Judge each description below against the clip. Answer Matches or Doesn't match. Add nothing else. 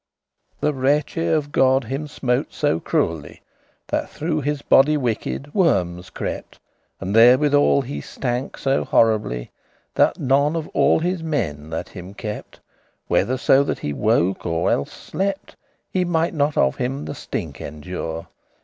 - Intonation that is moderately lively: Doesn't match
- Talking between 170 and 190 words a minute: Doesn't match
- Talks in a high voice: Doesn't match